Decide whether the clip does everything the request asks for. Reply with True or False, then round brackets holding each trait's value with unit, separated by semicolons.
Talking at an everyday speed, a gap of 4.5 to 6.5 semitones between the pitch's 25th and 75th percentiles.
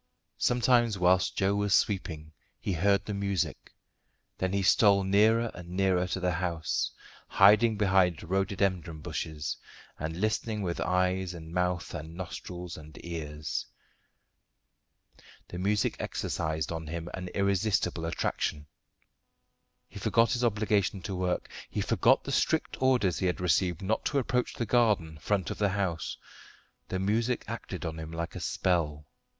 False (145 wpm; 3.4 semitones)